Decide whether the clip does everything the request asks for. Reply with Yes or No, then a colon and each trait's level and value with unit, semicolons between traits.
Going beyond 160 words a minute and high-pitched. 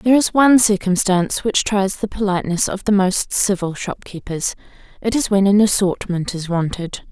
Yes: average, 170 wpm; high, 195 Hz